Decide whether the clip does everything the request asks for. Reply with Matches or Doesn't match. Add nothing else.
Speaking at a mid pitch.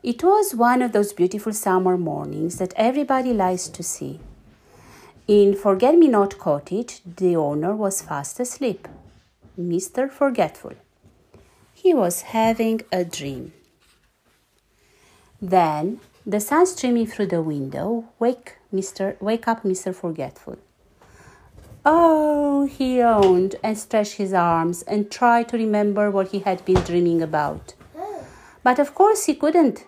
Doesn't match